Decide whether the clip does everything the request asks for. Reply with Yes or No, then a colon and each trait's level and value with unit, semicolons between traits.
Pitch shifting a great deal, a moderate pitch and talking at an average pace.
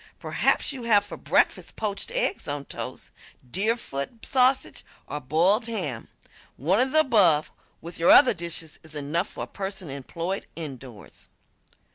Yes: wide, 7.2 semitones; medium, 175 Hz; average, 145 wpm